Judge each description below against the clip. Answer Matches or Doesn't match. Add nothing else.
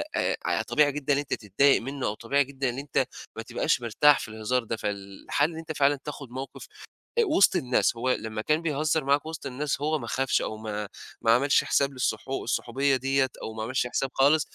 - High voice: Doesn't match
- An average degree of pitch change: Matches